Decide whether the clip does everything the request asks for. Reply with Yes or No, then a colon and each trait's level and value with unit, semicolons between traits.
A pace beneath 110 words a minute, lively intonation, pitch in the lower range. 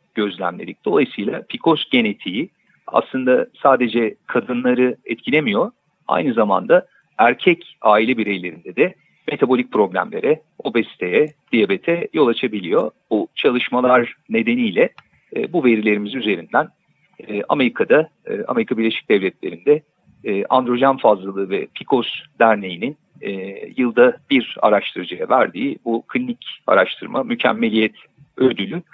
Yes: average, 100 wpm; wide, 8.4 semitones; low, 130 Hz